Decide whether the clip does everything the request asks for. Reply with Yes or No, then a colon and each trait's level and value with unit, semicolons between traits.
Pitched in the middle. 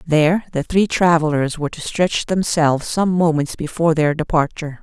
Yes: medium, 160 Hz